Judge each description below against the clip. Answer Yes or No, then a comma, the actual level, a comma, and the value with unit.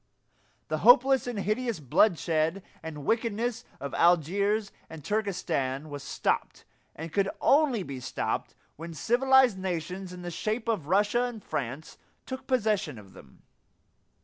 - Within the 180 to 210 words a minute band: No, slow, 135 wpm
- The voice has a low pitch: No, high, 195 Hz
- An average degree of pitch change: No, wide, 6.5 semitones